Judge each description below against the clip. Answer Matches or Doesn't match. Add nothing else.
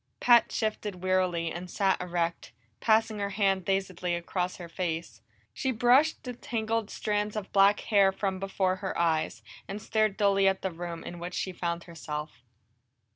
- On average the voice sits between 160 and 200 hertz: Matches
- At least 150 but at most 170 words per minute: Matches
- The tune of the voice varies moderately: Matches